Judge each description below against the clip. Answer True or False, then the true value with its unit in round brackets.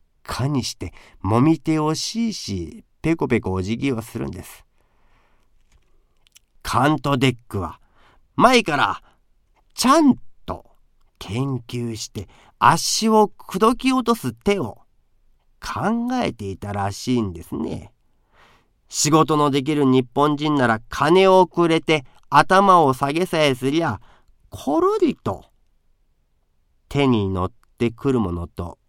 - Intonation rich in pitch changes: True (7.6 semitones)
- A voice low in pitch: True (130 Hz)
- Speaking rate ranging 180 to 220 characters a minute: True (215 characters per minute)